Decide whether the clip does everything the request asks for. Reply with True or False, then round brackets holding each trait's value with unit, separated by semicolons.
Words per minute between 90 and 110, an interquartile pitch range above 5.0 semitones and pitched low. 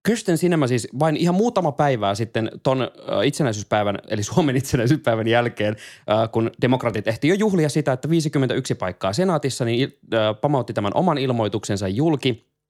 False (140 wpm; 5.4 semitones; 130 Hz)